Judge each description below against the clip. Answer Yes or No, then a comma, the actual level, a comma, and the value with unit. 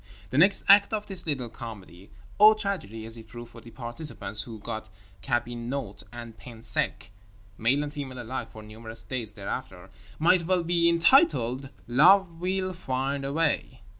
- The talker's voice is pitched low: Yes, low, 125 Hz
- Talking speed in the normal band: Yes, average, 155 wpm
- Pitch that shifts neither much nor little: No, wide, 6.9 semitones